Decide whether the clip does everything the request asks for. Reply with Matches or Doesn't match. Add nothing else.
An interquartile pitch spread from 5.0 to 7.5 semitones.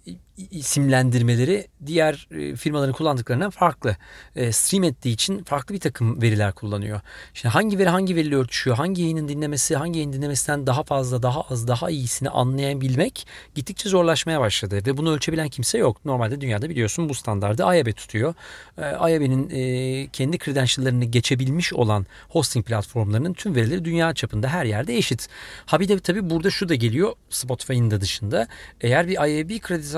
Matches